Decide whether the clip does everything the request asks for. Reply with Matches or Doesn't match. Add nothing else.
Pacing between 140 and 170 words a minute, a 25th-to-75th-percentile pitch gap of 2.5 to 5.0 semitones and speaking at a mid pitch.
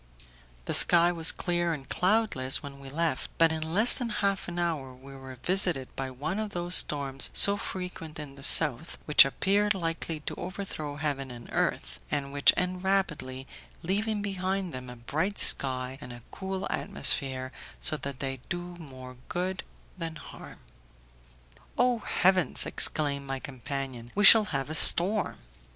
Doesn't match